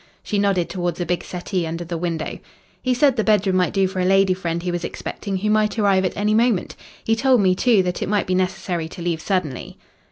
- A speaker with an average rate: No, fast, 235 wpm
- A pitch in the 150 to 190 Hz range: Yes, medium, 185 Hz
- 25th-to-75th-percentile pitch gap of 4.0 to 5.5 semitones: No, average, 2.9 semitones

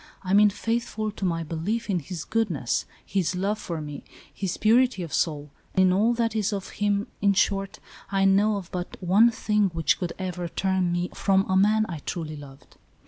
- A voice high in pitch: Yes, high, 195 Hz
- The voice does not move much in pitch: No, average, 3.3 semitones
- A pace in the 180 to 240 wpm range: Yes, average, 195 wpm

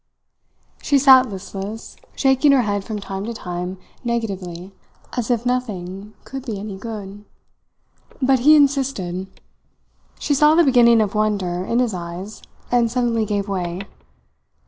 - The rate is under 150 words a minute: Yes, average, 140 wpm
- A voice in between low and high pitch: No, high, 215 Hz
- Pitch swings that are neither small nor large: Yes, average, 4.6 semitones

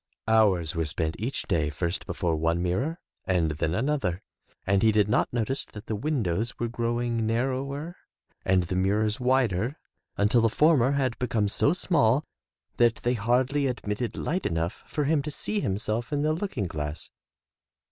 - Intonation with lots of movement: Yes, wide, 6.1 semitones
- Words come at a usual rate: Yes, average, 165 wpm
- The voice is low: Yes, low, 115 Hz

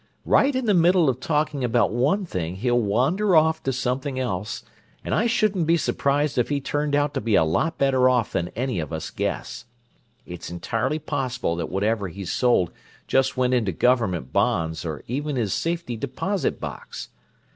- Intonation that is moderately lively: No, wide, 6.4 semitones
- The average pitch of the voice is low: Yes, low, 125 Hz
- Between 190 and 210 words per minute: No, average, 180 wpm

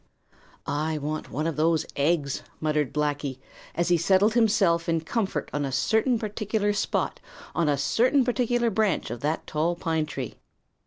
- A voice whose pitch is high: No, medium, 165 Hz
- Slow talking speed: No, average, 160 wpm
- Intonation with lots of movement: Yes, wide, 5.9 semitones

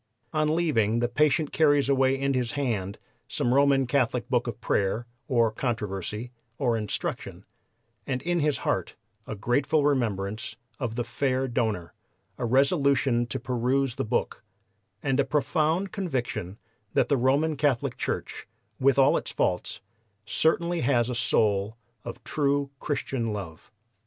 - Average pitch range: Yes, average, 3.6 semitones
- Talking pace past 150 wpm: No, average, 140 wpm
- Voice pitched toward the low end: Yes, low, 130 Hz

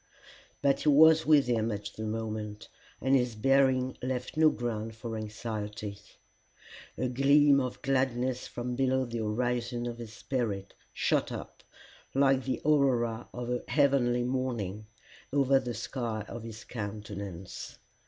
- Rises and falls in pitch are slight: No, average, 3.3 semitones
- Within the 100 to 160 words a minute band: Yes, average, 140 wpm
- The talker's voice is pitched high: No, low, 120 Hz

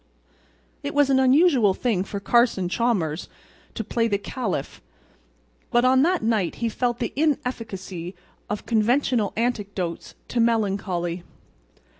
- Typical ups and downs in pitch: Yes, average, 4.4 semitones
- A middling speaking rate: No, slow, 125 wpm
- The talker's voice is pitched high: Yes, high, 230 Hz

